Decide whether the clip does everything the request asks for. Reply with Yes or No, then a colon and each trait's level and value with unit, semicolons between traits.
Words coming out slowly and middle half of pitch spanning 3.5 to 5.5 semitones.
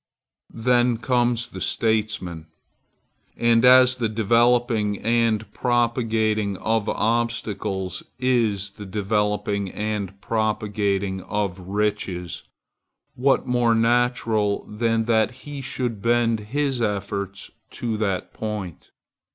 No: slow, 100 wpm; average, 2.7 semitones